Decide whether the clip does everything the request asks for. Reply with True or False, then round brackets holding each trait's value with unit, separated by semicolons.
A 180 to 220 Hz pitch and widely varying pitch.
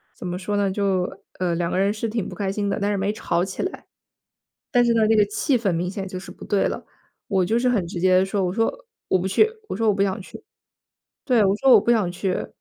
False (200 Hz; 2.9 semitones)